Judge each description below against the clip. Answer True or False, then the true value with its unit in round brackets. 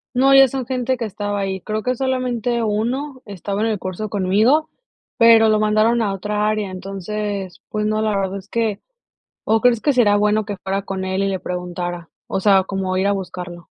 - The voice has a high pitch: True (210 Hz)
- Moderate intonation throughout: True (3.1 semitones)